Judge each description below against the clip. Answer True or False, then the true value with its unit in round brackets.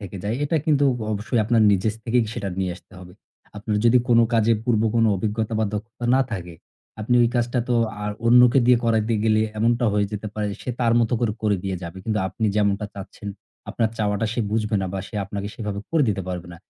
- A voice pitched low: True (110 Hz)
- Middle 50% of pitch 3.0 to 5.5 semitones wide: False (2.4 semitones)